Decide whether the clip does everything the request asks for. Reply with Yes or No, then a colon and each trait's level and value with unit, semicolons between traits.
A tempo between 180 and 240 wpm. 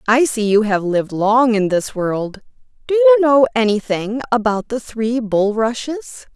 No: average, 160 wpm